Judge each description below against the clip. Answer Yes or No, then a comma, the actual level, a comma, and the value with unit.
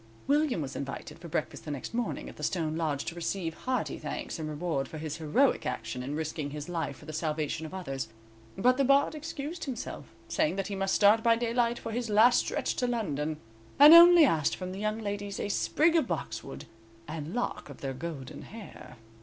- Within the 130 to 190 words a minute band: No, fast, 205 wpm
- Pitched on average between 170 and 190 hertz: Yes, medium, 185 Hz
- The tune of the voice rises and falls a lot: Yes, wide, 7.8 semitones